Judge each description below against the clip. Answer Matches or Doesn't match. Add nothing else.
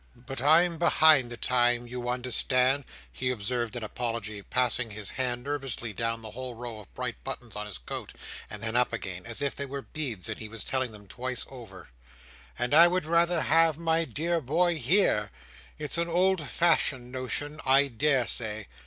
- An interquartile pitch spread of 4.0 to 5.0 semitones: Matches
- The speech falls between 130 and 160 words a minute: Doesn't match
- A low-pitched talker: Matches